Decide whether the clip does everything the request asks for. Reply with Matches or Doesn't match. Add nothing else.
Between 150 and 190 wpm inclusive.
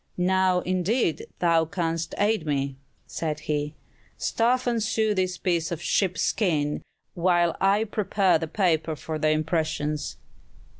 Doesn't match